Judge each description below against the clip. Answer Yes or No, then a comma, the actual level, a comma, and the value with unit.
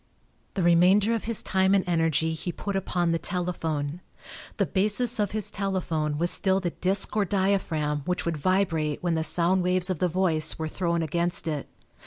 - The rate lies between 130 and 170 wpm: No, average, 185 wpm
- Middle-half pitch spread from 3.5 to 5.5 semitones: No, average, 2.9 semitones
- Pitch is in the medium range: Yes, medium, 180 Hz